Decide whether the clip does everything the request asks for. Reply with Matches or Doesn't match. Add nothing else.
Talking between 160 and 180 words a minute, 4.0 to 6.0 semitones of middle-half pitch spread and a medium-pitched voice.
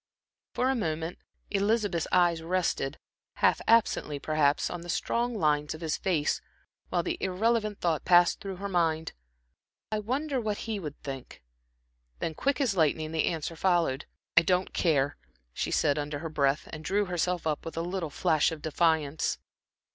Matches